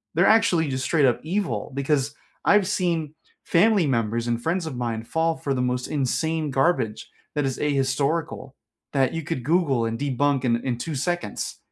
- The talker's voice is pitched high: No, medium, 140 Hz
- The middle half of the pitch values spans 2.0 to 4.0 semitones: No, average, 4.5 semitones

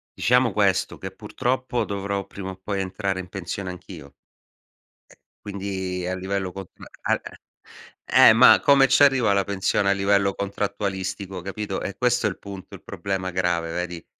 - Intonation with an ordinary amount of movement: No, narrow, 1.6 semitones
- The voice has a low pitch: Yes, low, 100 Hz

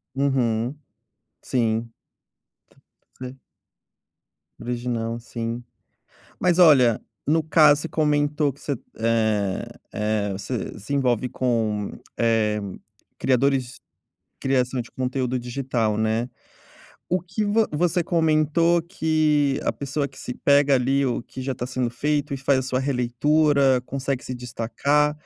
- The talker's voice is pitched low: Yes, low, 130 Hz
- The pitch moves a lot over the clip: No, average, 3.8 semitones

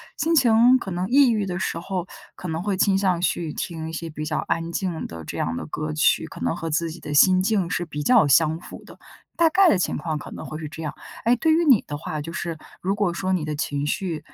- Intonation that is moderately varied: Yes, average, 4.1 semitones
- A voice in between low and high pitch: Yes, medium, 170 Hz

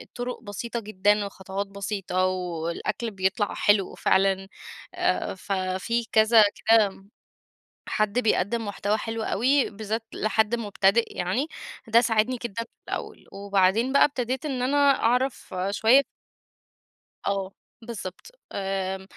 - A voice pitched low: No, high, 210 Hz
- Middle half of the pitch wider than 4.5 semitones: No, average, 3.3 semitones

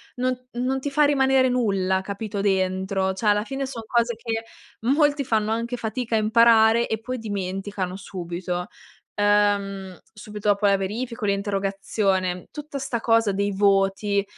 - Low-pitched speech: No, high, 210 Hz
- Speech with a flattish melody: No, average, 3.4 semitones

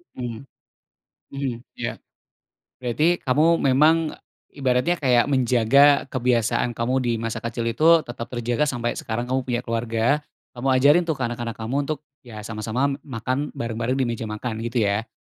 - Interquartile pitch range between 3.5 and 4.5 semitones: No, average, 2.7 semitones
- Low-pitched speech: Yes, low, 120 Hz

